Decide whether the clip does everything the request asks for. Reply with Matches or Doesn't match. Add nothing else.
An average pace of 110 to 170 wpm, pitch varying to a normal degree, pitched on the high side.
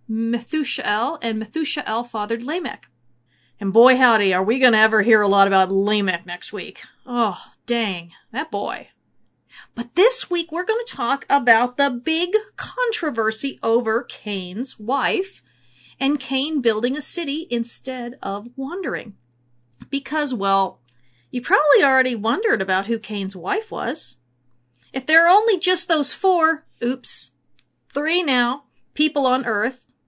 Doesn't match